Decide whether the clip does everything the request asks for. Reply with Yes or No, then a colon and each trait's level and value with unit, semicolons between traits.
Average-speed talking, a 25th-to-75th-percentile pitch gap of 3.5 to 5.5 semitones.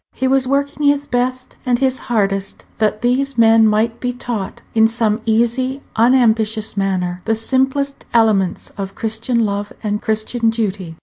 No: average, 150 wpm; average, 3.1 semitones